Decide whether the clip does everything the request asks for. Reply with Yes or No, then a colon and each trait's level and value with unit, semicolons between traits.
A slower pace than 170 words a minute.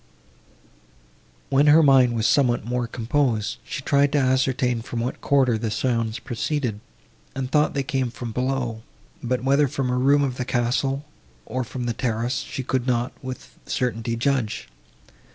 Yes: average, 160 wpm